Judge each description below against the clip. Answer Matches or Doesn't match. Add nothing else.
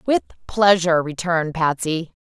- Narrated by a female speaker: Matches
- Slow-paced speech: Matches